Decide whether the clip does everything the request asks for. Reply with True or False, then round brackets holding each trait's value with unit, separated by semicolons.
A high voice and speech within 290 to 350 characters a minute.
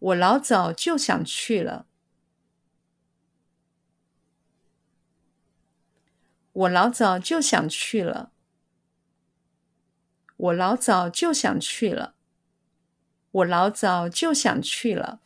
False (215 Hz; 110 characters per minute)